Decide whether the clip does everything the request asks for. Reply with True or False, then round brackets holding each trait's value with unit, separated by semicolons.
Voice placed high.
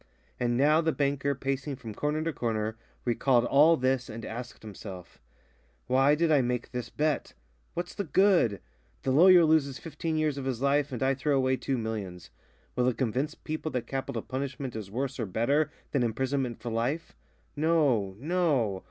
False (135 Hz)